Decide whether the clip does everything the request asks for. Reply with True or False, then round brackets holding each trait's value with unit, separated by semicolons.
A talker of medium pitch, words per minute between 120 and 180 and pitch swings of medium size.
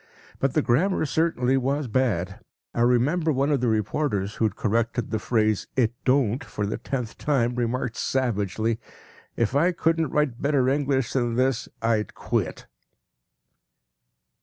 False (125 Hz; 145 wpm; 3.6 semitones)